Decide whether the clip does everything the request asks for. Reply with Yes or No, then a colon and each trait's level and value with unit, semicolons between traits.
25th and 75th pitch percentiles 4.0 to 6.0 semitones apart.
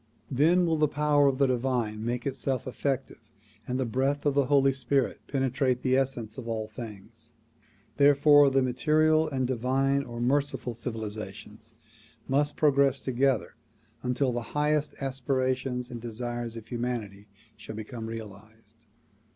No: average, 3.2 semitones